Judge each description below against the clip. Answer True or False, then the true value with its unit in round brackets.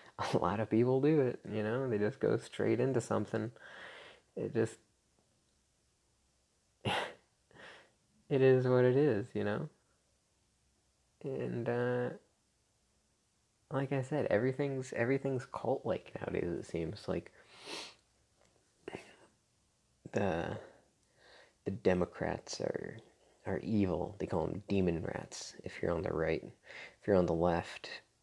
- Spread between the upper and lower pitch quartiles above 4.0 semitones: True (4.8 semitones)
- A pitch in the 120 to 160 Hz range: False (110 Hz)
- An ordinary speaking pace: False (120 wpm)